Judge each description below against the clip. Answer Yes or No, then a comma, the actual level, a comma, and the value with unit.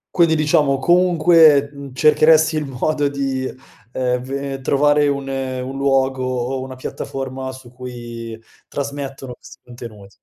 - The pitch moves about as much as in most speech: No, narrow, 2.2 semitones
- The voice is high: No, low, 135 Hz